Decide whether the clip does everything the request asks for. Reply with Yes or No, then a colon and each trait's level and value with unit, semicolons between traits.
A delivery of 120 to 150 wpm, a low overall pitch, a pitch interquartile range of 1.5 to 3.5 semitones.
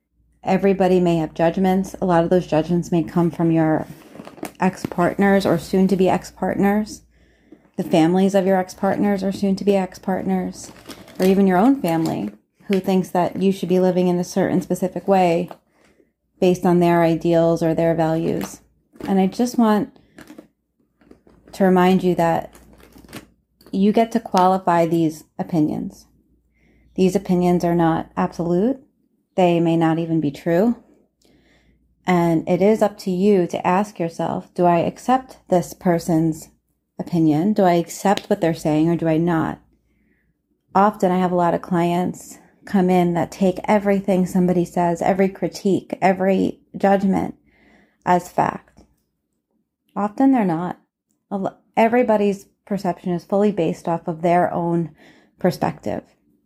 No: average, 140 wpm; medium, 180 Hz; narrow, 2.5 semitones